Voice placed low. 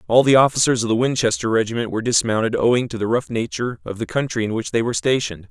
Yes: low, 115 Hz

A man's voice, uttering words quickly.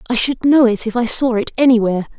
No: female; fast, 250 wpm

